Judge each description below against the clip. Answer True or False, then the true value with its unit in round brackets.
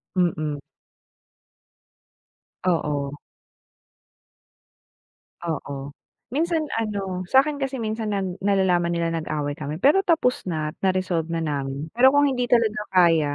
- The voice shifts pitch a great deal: True (7.3 semitones)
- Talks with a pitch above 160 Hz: True (185 Hz)